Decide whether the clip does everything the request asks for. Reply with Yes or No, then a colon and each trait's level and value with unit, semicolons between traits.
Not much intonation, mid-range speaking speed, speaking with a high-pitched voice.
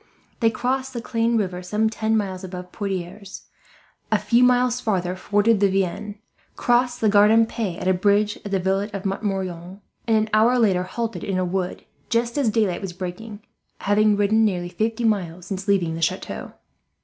No: average, 3.2 semitones; average, 175 wpm; high, 205 Hz